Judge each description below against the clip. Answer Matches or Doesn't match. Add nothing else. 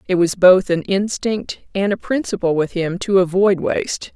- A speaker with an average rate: Matches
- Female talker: Matches